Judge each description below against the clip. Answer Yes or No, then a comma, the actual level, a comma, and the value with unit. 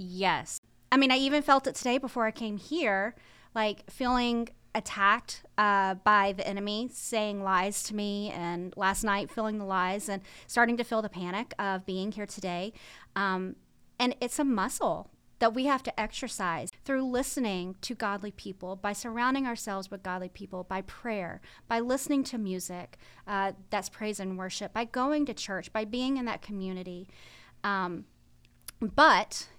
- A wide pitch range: No, average, 4.0 semitones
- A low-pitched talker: No, high, 205 Hz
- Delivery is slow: No, average, 165 wpm